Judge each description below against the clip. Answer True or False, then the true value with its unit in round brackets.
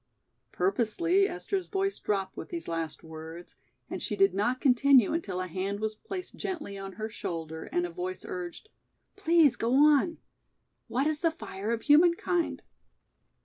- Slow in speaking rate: False (155 wpm)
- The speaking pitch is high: True (235 Hz)